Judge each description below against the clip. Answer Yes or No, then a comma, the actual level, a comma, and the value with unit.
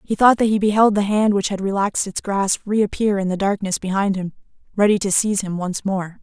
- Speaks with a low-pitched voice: No, high, 200 Hz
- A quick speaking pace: Yes, fast, 230 wpm